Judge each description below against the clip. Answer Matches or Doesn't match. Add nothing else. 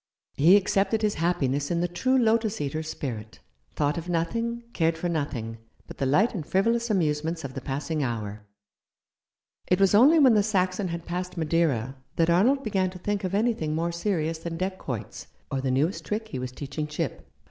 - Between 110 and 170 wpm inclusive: Doesn't match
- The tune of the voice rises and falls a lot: Matches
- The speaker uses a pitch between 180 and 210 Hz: Doesn't match